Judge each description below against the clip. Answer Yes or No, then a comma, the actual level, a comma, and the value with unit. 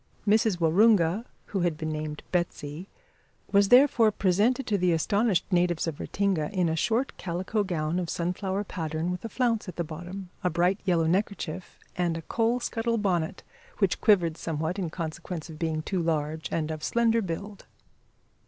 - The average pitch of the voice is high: No, medium, 180 Hz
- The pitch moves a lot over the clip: No, average, 3.9 semitones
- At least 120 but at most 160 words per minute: No, average, 170 wpm